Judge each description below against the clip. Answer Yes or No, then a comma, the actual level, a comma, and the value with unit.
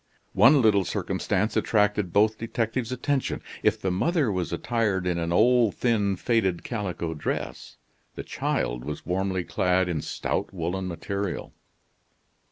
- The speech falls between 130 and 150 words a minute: Yes, slow, 135 wpm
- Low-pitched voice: Yes, low, 100 Hz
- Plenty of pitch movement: No, average, 4.1 semitones